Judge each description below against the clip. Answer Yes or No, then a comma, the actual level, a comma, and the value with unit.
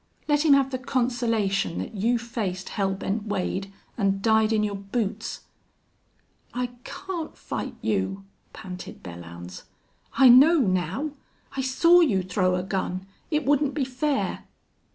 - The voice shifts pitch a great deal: Yes, wide, 6.0 semitones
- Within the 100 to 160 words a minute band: Yes, average, 140 wpm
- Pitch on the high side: Yes, high, 220 Hz